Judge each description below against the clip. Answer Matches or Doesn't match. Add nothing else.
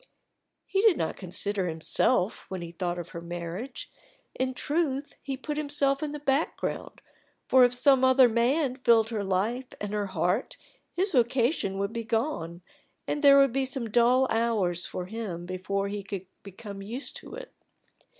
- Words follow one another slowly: Doesn't match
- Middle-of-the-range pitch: Doesn't match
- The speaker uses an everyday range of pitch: Doesn't match